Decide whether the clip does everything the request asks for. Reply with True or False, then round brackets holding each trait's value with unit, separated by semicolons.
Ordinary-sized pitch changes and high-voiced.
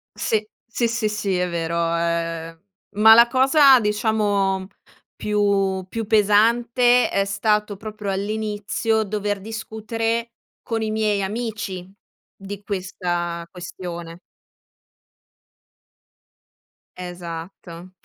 True (3.3 semitones; 205 Hz)